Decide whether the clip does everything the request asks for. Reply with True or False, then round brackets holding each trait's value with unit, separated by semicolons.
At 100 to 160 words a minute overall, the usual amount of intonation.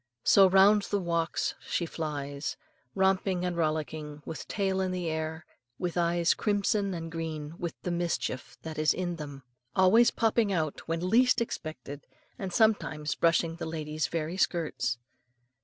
True (150 wpm; 3.4 semitones)